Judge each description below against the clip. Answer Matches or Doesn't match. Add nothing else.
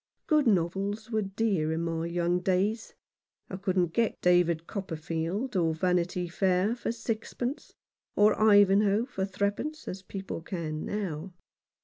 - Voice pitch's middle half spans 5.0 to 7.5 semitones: Doesn't match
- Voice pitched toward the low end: Doesn't match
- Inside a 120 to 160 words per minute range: Matches